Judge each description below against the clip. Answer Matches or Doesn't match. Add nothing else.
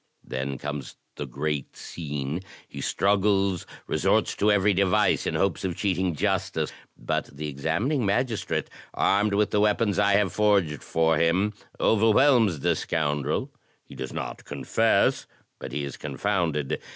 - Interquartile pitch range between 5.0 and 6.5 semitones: Matches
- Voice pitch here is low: Matches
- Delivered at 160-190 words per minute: Doesn't match